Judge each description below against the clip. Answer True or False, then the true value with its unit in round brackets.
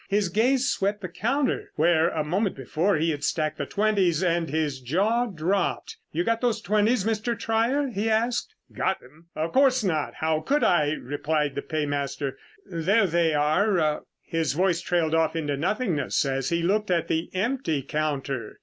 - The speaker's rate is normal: True (170 wpm)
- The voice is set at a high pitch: False (170 Hz)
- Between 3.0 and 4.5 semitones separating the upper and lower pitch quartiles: False (5.6 semitones)